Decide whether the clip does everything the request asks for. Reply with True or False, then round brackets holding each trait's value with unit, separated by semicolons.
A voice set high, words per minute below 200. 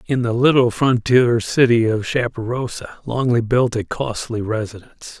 False (120 Hz; 140 wpm)